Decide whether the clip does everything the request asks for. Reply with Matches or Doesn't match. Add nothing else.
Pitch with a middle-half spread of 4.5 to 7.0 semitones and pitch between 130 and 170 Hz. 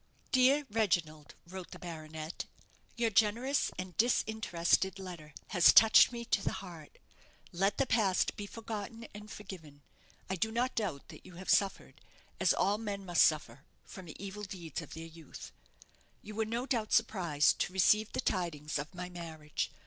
Doesn't match